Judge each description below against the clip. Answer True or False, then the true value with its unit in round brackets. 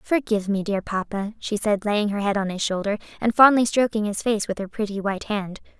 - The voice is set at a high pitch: True (210 Hz)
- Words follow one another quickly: True (230 wpm)